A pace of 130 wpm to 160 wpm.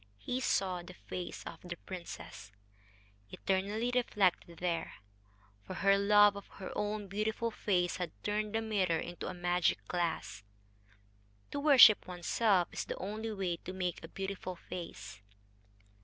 Yes: average, 140 wpm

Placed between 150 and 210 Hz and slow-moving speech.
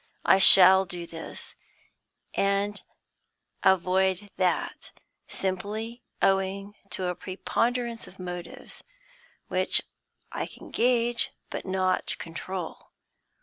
Yes: high, 190 Hz; slow, 95 wpm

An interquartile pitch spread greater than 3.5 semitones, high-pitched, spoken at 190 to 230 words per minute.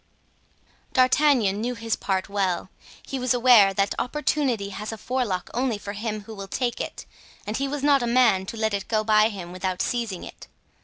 Yes: average, 4.0 semitones; high, 220 Hz; average, 195 wpm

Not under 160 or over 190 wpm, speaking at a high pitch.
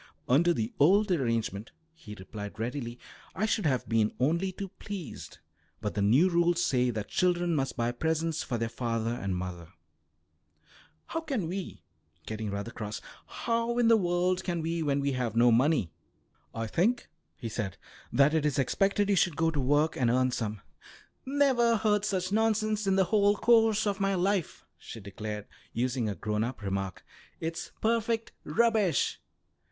No: average, 170 wpm; medium, 155 Hz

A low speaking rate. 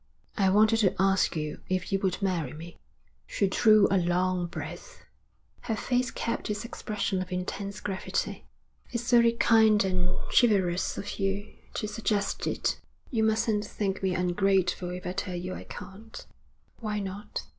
No: average, 155 wpm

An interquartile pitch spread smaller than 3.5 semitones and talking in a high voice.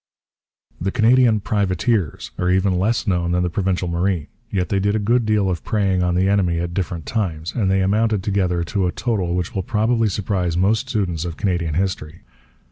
No: average, 3.1 semitones; very low, 95 Hz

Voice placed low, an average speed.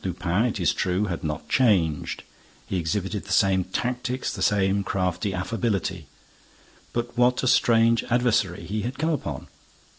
Yes: low, 100 Hz; average, 150 wpm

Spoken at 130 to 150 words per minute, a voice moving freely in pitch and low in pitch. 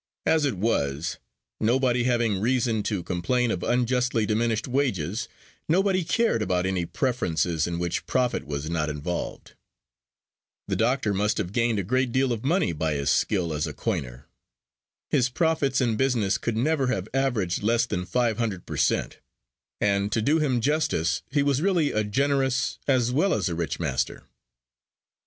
No: average, 165 wpm; wide, 6.6 semitones; low, 115 Hz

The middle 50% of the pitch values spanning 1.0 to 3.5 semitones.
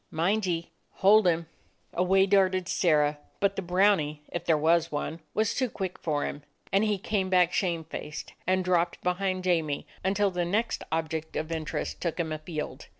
Yes: average, 3.1 semitones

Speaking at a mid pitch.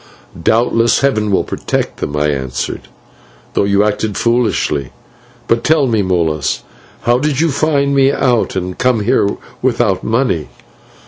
No: low, 115 Hz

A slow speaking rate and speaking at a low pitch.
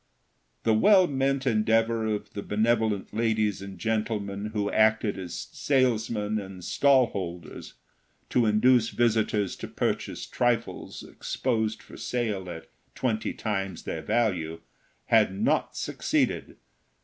Yes: slow, 120 wpm; low, 110 Hz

